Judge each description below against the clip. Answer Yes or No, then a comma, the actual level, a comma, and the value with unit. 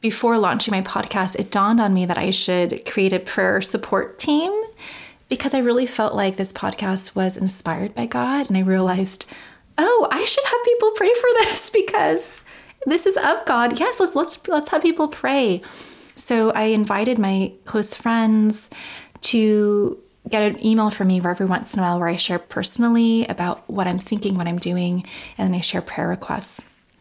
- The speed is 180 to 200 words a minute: Yes, average, 185 wpm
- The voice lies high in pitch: Yes, high, 215 Hz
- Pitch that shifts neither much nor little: No, wide, 6.6 semitones